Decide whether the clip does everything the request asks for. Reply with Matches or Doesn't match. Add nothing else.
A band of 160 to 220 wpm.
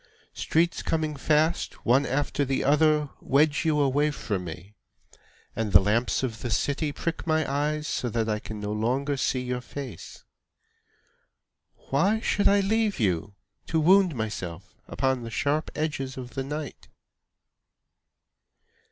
Doesn't match